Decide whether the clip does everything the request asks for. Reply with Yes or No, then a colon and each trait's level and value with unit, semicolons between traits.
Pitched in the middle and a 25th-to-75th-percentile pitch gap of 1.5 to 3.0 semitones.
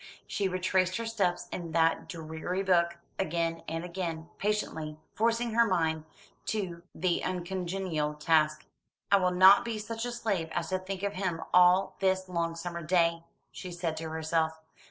Yes: medium, 180 Hz; narrow, 2.6 semitones